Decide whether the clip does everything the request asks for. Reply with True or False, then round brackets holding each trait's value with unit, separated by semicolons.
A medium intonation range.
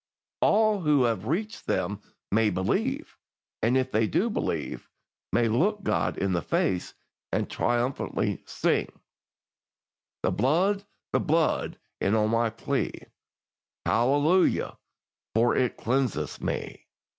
False (8.4 semitones)